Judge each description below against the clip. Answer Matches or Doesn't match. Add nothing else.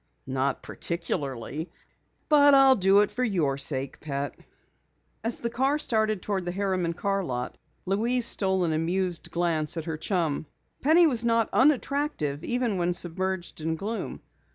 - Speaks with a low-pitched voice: Doesn't match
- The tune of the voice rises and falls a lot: Matches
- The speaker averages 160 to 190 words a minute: Doesn't match